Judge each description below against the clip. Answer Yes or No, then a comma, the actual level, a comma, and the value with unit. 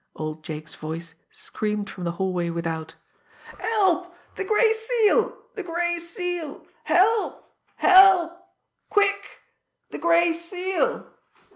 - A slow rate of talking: Yes, slow, 110 wpm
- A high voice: Yes, very high, 345 Hz